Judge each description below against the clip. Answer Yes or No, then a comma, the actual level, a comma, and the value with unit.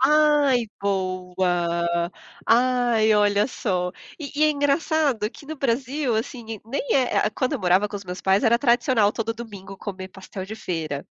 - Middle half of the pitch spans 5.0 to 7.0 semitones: Yes, wide, 5.5 semitones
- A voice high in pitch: Yes, high, 220 Hz